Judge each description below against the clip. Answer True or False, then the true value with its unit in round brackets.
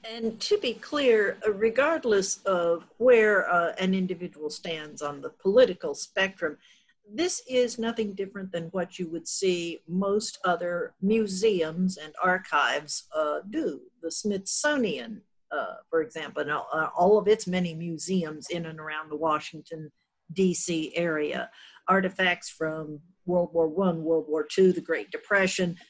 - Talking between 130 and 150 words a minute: True (145 wpm)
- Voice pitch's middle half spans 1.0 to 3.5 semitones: False (4.5 semitones)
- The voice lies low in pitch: False (185 Hz)